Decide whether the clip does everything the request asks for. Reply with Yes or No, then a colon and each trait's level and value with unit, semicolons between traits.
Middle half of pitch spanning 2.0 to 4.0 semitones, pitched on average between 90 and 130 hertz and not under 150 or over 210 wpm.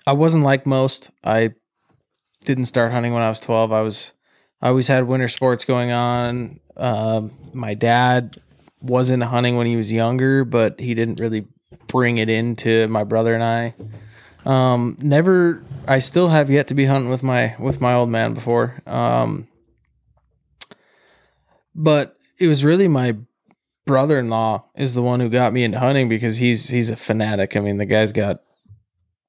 Yes: average, 2.8 semitones; low, 120 Hz; average, 170 wpm